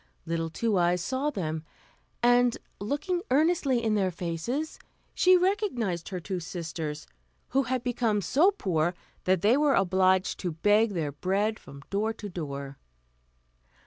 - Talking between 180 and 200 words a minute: No, average, 145 wpm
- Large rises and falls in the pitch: Yes, wide, 6.7 semitones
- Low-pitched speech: No, high, 200 Hz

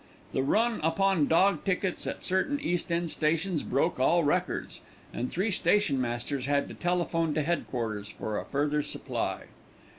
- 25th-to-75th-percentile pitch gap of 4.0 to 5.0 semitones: Yes, average, 4.4 semitones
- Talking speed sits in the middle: Yes, average, 150 wpm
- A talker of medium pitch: Yes, medium, 165 Hz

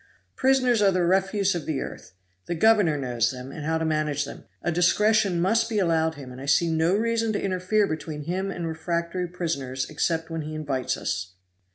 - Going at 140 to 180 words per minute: No, average, 200 wpm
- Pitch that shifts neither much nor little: Yes, average, 4.5 semitones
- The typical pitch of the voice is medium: Yes, medium, 170 Hz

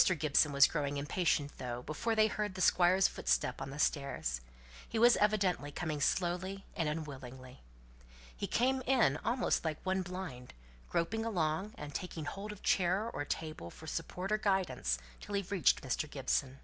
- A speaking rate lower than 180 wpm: Yes, average, 165 wpm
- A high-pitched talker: No, medium, 165 Hz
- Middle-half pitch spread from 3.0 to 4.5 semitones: No, wide, 5.6 semitones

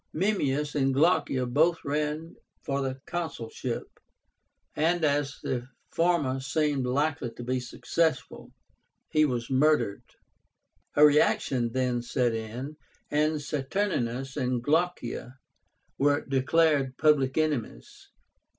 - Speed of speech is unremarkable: No, slow, 105 wpm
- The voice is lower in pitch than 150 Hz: Yes, medium, 140 Hz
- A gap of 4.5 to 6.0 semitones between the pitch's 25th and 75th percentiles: No, average, 3.2 semitones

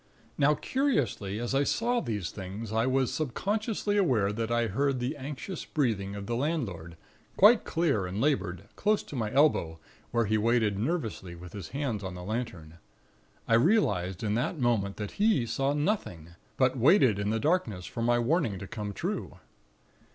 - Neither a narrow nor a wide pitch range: No, wide, 6.4 semitones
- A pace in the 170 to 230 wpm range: Yes, average, 175 wpm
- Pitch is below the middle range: Yes, low, 115 Hz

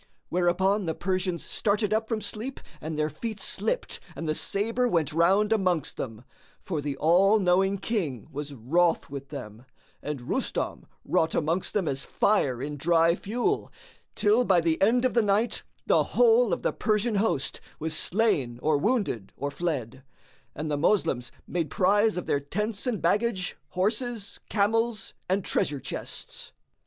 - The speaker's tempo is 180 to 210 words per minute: No, average, 160 wpm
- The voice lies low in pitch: No, medium, 185 Hz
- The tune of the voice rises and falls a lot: Yes, wide, 6.0 semitones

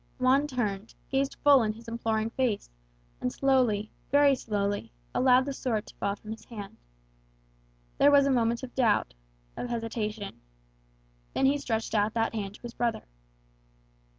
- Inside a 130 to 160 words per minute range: Yes, average, 155 wpm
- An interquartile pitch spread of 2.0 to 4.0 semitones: Yes, average, 3.6 semitones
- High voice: Yes, high, 230 Hz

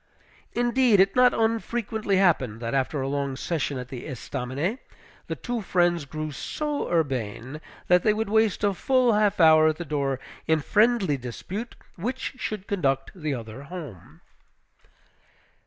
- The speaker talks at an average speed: Yes, average, 150 wpm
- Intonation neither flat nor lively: No, wide, 7.8 semitones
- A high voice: No, medium, 170 Hz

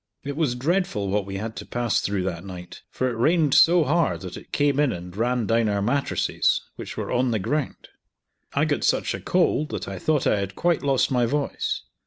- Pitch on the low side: Yes, low, 125 Hz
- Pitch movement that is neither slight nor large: No, wide, 6.5 semitones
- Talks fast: Yes, fast, 220 wpm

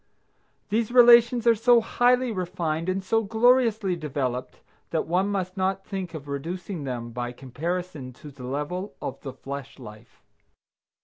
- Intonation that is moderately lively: No, wide, 7.5 semitones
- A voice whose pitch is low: No, medium, 180 Hz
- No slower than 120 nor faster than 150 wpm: Yes, average, 145 wpm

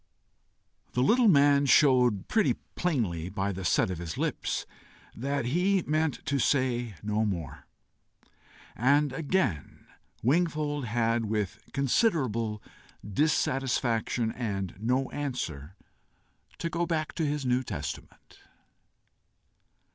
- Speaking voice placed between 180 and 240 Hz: No, low, 125 Hz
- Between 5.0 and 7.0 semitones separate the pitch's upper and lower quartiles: Yes, wide, 5.6 semitones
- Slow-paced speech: Yes, slow, 110 wpm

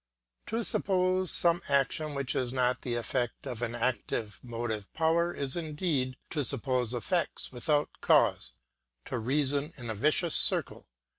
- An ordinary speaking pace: Yes, average, 145 wpm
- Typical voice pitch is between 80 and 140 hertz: Yes, low, 135 Hz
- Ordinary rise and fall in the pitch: Yes, average, 4.7 semitones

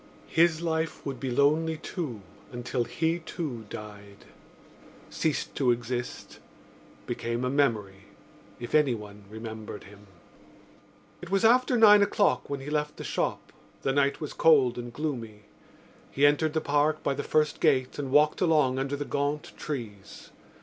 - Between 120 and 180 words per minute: Yes, average, 145 wpm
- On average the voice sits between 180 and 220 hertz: No, medium, 140 Hz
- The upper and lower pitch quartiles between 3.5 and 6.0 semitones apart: Yes, average, 4.6 semitones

